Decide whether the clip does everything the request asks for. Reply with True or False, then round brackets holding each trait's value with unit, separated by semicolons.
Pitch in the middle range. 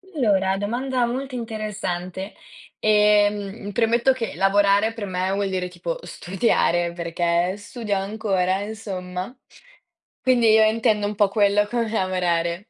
False (205 Hz)